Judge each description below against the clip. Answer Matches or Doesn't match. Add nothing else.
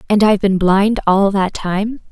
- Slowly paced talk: Doesn't match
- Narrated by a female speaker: Matches